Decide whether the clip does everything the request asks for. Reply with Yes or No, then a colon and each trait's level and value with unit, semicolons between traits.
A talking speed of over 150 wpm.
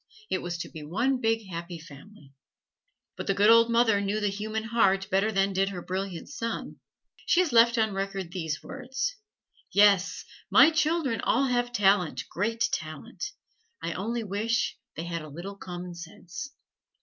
Yes: average, 160 wpm